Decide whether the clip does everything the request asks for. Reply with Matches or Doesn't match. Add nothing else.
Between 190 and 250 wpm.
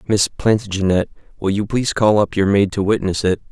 Matches